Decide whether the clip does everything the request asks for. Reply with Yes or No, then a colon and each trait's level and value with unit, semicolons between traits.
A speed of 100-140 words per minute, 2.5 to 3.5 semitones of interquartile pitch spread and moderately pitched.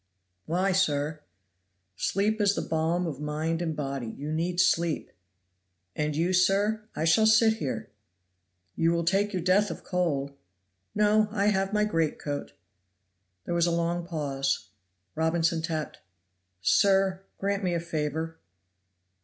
No: slow, 135 wpm; average, 3.9 semitones; medium, 170 Hz